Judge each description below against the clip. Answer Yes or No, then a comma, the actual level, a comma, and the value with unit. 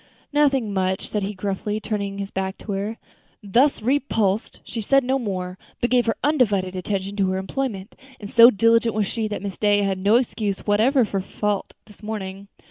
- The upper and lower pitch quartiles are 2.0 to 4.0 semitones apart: Yes, average, 2.9 semitones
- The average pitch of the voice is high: Yes, high, 210 Hz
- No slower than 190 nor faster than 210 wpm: Yes, average, 195 wpm